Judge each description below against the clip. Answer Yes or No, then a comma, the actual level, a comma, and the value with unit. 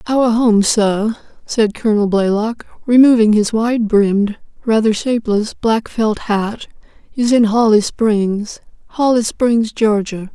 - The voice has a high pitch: Yes, high, 220 Hz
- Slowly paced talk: Yes, slow, 120 wpm